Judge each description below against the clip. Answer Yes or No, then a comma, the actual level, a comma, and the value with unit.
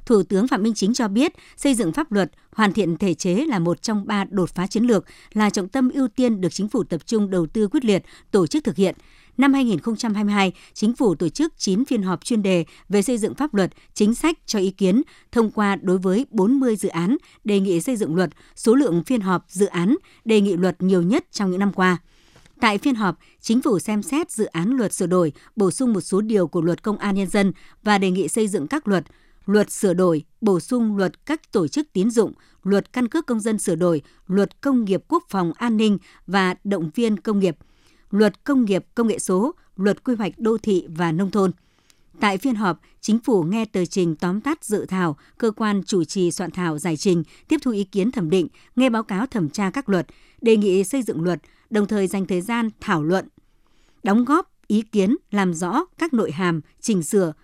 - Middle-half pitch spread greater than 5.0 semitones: No, average, 3.9 semitones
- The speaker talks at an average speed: Yes, average, 230 wpm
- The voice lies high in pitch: Yes, high, 205 Hz